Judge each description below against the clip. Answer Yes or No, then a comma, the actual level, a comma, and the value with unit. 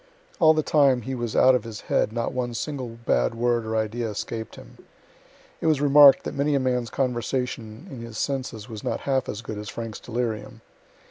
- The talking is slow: No, average, 200 wpm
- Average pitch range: Yes, average, 3.1 semitones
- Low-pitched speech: Yes, low, 120 Hz